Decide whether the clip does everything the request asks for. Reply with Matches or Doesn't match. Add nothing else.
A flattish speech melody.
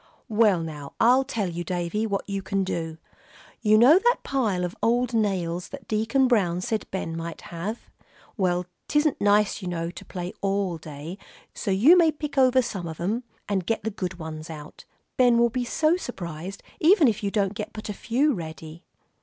Doesn't match